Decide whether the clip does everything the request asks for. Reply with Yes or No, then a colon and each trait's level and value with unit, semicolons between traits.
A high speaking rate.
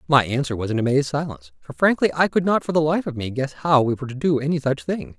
Yes: fast, 290 wpm